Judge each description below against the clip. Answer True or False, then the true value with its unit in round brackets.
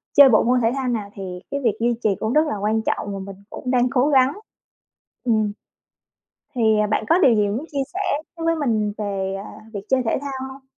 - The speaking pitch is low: False (230 Hz)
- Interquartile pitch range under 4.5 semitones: True (4.1 semitones)